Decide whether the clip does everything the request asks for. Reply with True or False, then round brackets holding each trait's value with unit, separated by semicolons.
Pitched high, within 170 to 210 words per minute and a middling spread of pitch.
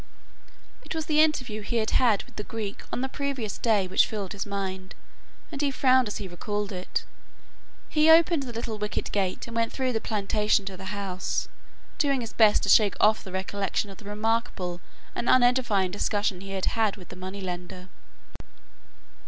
True (210 Hz; 185 wpm; 3.8 semitones)